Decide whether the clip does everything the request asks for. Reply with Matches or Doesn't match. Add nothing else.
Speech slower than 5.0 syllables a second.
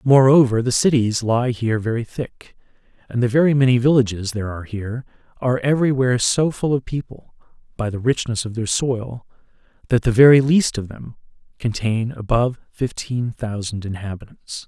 Doesn't match